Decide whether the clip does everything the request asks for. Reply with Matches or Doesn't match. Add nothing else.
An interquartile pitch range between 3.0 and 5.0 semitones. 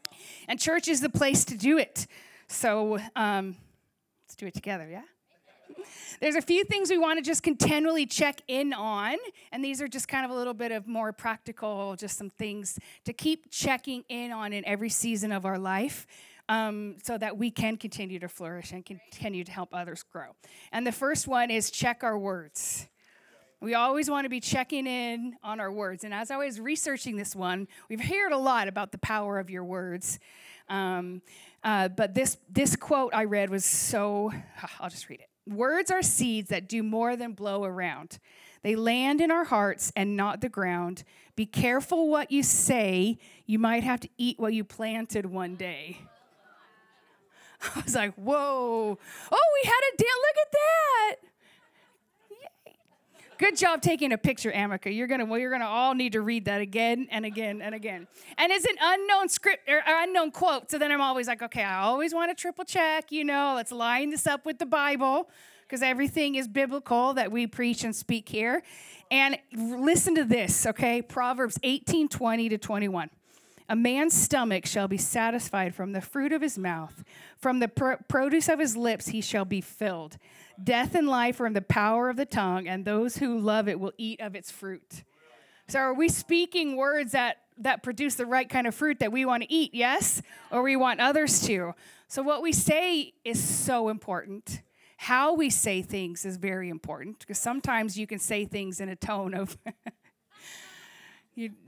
Doesn't match